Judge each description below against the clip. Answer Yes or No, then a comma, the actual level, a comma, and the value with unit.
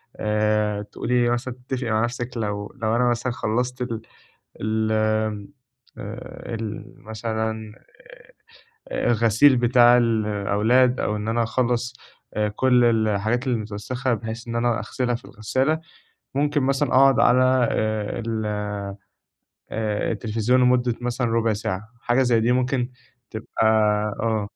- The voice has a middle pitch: No, low, 115 Hz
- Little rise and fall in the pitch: Yes, narrow, 2.3 semitones